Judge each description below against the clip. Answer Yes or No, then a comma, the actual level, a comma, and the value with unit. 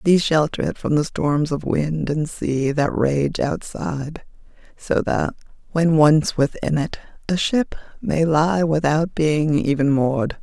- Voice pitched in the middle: Yes, medium, 150 Hz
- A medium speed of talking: Yes, average, 155 wpm